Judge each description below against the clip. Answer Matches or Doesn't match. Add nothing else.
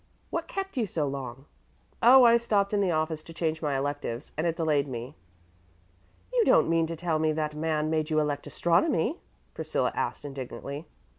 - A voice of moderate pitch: Matches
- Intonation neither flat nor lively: Matches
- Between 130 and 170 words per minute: Doesn't match